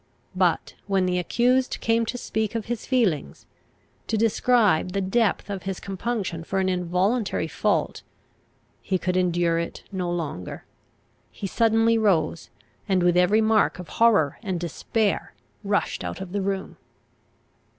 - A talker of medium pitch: No, high, 195 Hz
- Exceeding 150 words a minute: No, average, 145 wpm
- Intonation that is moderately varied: Yes, average, 3.8 semitones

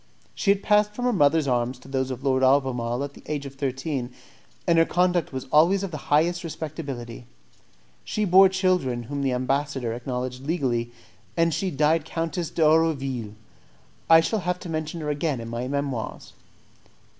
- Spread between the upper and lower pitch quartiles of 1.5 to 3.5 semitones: No, average, 4.4 semitones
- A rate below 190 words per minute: Yes, average, 170 wpm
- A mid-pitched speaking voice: Yes, medium, 145 Hz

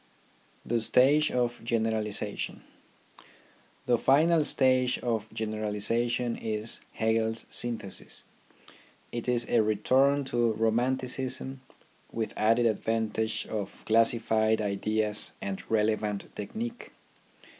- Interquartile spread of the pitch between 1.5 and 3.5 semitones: Yes, narrow, 2.4 semitones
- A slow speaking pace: Yes, slow, 100 wpm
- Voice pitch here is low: Yes, low, 115 Hz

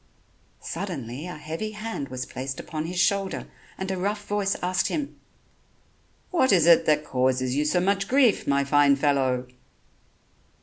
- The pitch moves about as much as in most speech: No, wide, 6.1 semitones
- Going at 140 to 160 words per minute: Yes, average, 150 wpm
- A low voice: No, medium, 165 Hz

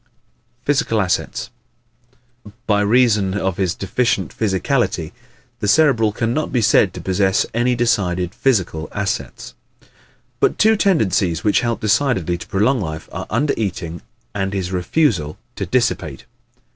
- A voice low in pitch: Yes, low, 100 Hz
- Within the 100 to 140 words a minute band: Yes, slow, 135 wpm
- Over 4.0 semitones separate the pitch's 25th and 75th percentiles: Yes, average, 4.5 semitones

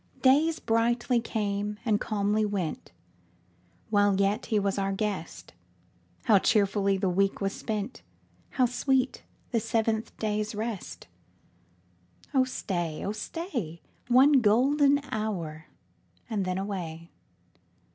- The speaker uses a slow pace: Yes, slow, 115 wpm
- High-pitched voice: Yes, high, 210 Hz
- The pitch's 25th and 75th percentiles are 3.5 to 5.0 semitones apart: No, average, 3.1 semitones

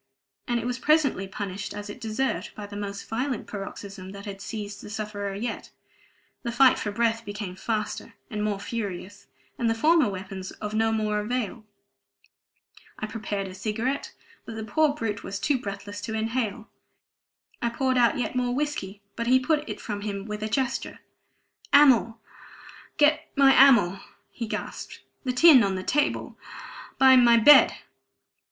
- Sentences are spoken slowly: No, average, 165 wpm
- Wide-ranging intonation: No, average, 3.7 semitones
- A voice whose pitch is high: Yes, high, 220 Hz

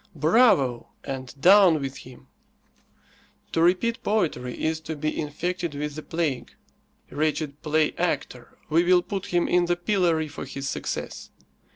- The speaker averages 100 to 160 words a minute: Yes, average, 140 wpm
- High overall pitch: No, medium, 160 Hz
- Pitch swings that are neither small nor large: Yes, average, 3.6 semitones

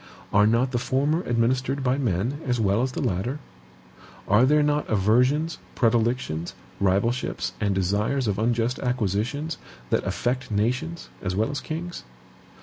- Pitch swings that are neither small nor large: Yes, average, 4.4 semitones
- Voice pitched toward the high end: No, low, 120 Hz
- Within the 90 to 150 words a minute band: Yes, average, 145 wpm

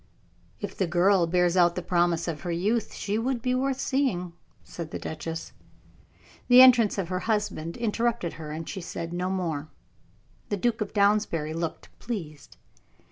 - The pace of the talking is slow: No, average, 165 wpm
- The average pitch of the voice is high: No, medium, 180 Hz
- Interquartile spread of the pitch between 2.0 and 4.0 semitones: No, average, 4.7 semitones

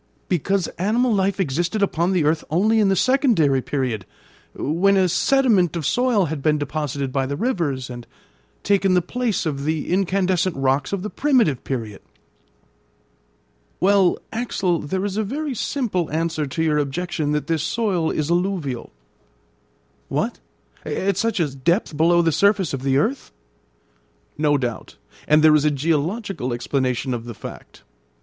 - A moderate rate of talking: Yes, average, 155 wpm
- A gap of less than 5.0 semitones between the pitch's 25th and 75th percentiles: No, wide, 5.6 semitones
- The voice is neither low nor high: Yes, medium, 170 Hz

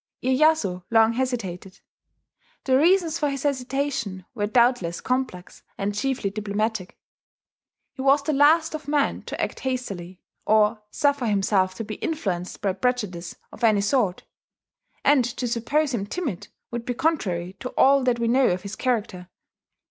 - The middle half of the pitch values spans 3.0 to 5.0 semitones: No, wide, 5.4 semitones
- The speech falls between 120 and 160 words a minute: Yes, average, 150 wpm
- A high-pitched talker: Yes, high, 235 Hz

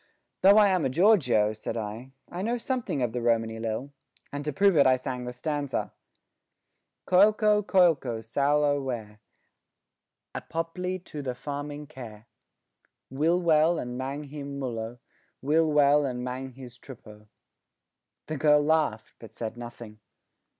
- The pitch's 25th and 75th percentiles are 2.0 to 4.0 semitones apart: No, average, 4.6 semitones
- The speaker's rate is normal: Yes, average, 145 wpm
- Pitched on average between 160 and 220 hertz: No, medium, 140 Hz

